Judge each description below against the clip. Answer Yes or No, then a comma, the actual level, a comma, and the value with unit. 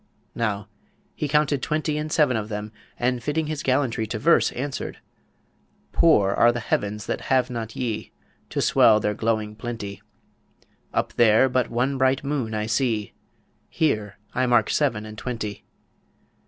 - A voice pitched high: No, low, 120 Hz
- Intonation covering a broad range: No, average, 4.1 semitones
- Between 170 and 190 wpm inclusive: No, average, 155 wpm